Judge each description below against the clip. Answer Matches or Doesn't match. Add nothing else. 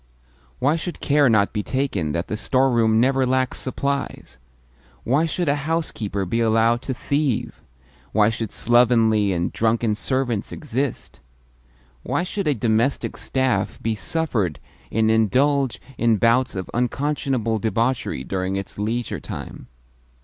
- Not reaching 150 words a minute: Matches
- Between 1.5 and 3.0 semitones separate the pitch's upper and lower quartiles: Doesn't match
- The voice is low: Matches